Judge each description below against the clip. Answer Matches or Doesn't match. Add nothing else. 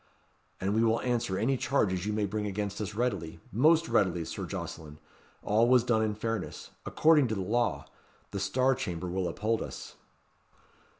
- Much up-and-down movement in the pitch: Doesn't match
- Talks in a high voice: Doesn't match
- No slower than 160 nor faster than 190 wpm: Matches